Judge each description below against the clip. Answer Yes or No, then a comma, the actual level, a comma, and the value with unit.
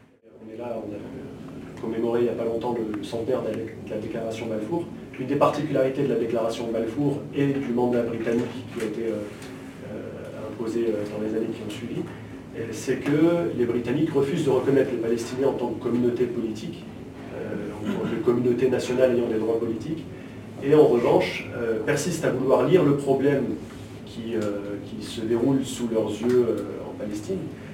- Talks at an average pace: Yes, average, 165 wpm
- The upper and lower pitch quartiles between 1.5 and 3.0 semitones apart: Yes, narrow, 2.5 semitones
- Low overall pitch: Yes, low, 120 Hz